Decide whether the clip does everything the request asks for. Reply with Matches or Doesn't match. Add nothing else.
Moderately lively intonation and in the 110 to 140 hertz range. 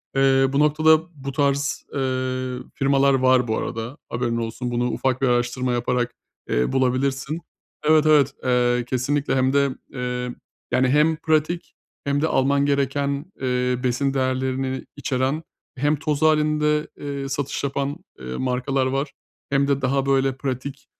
Doesn't match